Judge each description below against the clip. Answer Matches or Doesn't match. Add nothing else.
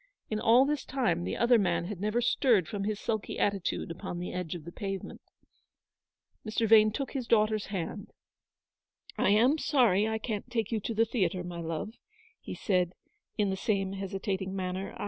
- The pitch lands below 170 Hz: Doesn't match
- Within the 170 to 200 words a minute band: Matches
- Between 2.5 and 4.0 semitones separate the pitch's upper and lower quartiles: Matches